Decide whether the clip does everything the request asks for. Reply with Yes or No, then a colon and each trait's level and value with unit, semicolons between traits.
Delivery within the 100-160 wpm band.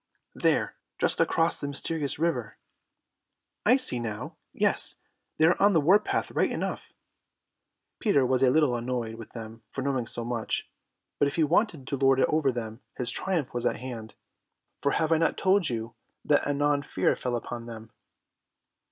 No: average, 175 wpm